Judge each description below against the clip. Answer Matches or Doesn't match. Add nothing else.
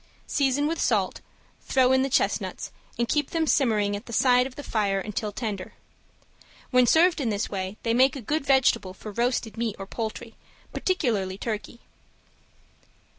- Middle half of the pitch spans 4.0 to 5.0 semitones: Matches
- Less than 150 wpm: Doesn't match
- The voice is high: Matches